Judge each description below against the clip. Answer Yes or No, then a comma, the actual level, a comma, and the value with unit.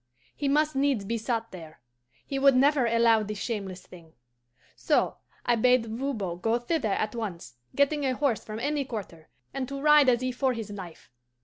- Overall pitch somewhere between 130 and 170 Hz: No, high, 235 Hz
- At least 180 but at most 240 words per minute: Yes, average, 185 wpm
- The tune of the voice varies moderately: Yes, average, 4.5 semitones